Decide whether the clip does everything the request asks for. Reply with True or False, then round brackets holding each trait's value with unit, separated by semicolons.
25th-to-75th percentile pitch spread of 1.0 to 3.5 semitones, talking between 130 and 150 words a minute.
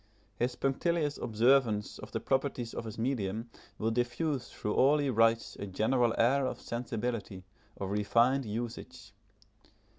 True (3.1 semitones; 140 wpm)